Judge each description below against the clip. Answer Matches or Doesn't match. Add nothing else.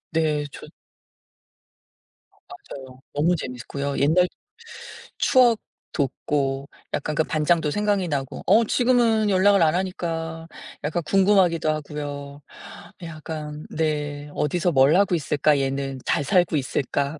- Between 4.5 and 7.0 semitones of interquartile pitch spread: Doesn't match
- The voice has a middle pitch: Matches